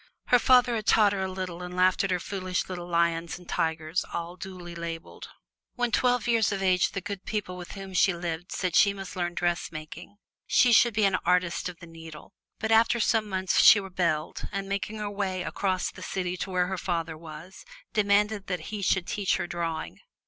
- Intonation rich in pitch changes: No, average, 2.7 semitones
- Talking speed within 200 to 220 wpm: Yes, fast, 205 wpm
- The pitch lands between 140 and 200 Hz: Yes, medium, 185 Hz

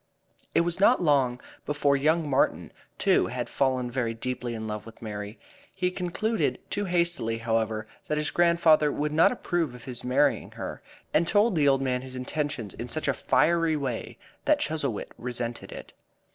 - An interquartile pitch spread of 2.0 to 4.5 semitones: No, wide, 5.5 semitones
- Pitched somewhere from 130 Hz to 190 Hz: Yes, medium, 140 Hz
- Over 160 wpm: Yes, average, 175 wpm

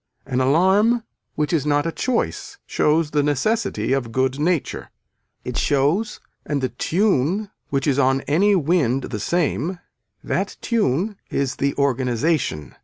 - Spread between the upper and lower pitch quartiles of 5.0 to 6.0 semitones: Yes, wide, 5.5 semitones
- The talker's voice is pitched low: No, medium, 145 Hz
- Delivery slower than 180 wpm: Yes, average, 140 wpm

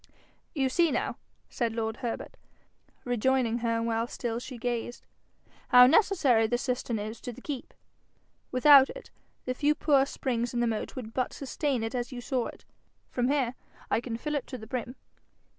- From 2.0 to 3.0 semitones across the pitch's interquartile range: Yes, narrow, 2.4 semitones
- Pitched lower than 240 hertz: No, high, 245 Hz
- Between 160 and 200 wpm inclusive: Yes, average, 175 wpm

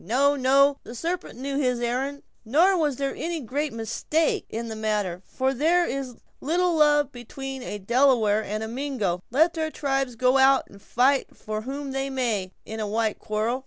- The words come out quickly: No, average, 190 wpm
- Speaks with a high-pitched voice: Yes, very high, 265 Hz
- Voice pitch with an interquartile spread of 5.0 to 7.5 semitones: No, average, 4.1 semitones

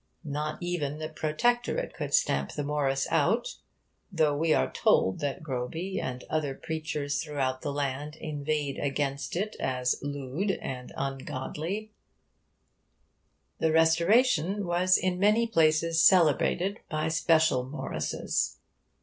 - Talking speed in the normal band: No, slow, 120 wpm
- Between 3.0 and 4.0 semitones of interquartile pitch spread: Yes, average, 3.6 semitones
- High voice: No, medium, 155 Hz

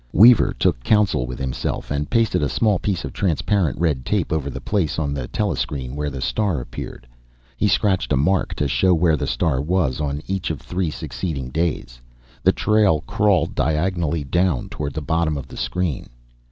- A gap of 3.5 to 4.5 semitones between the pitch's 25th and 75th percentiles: No, average, 5.1 semitones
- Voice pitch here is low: Yes, very low, 80 Hz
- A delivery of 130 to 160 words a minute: No, average, 185 wpm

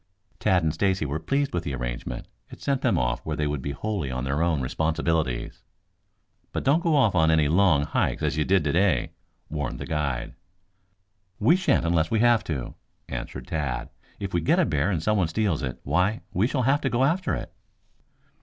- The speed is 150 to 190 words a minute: No, average, 200 wpm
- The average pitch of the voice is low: Yes, very low, 80 Hz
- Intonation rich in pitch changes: Yes, wide, 6.5 semitones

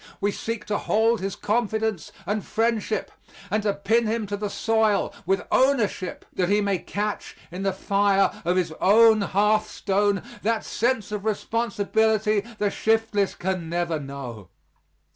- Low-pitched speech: No, high, 205 Hz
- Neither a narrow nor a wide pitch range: No, narrow, 2.2 semitones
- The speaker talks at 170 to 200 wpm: No, average, 145 wpm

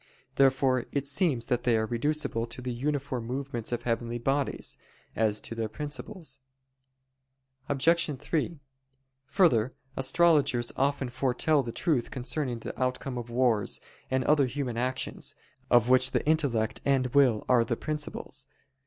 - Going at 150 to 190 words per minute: No, average, 140 wpm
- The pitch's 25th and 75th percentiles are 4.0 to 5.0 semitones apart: No, average, 3.1 semitones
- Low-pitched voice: Yes, low, 130 Hz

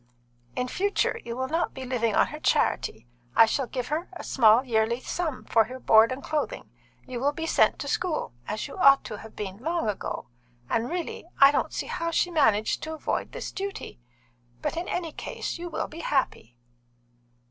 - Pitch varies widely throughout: Yes, wide, 6.2 semitones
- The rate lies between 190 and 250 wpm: Yes, average, 195 wpm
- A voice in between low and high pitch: No, very high, 265 Hz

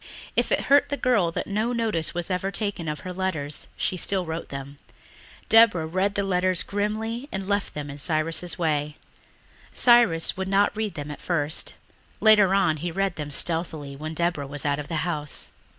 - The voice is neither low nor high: Yes, medium, 175 Hz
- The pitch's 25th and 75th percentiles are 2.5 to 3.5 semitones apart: No, average, 4.7 semitones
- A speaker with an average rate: Yes, average, 190 wpm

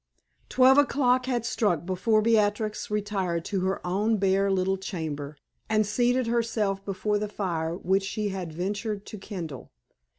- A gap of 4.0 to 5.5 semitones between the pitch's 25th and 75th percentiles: No, average, 2.8 semitones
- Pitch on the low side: No, high, 200 Hz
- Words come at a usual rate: Yes, average, 145 wpm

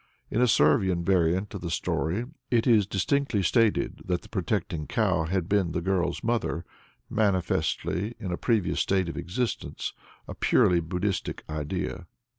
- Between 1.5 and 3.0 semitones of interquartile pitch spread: No, average, 3.5 semitones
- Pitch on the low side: Yes, very low, 95 Hz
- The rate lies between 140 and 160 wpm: Yes, average, 150 wpm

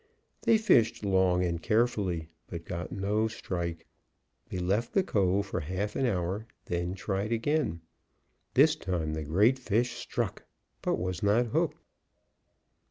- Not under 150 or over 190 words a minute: No, average, 140 wpm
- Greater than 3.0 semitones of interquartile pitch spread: Yes, average, 4.2 semitones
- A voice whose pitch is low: Yes, very low, 95 Hz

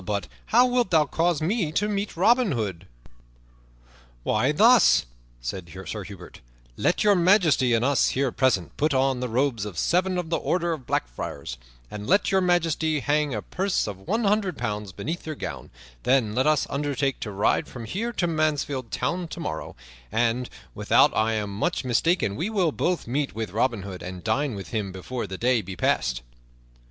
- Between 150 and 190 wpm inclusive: Yes, average, 185 wpm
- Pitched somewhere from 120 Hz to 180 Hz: Yes, low, 135 Hz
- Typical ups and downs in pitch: No, wide, 8.4 semitones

